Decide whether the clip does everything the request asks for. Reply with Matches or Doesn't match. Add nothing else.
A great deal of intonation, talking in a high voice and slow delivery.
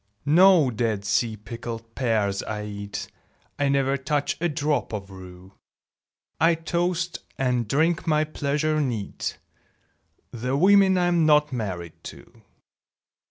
Doesn't match